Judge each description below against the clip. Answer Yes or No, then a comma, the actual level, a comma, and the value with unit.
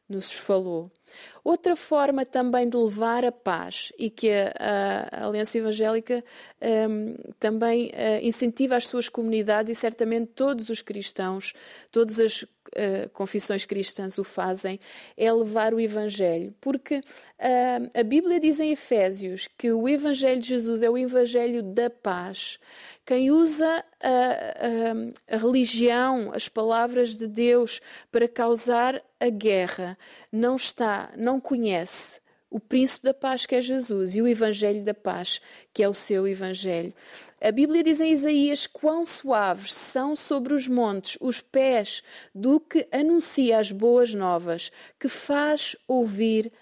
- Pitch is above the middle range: Yes, high, 235 Hz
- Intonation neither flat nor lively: Yes, average, 3.6 semitones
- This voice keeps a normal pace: Yes, average, 145 wpm